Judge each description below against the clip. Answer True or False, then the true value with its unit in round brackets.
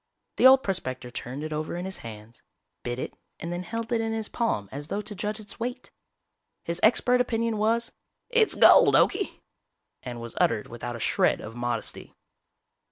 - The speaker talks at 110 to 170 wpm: False (180 wpm)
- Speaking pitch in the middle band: True (180 Hz)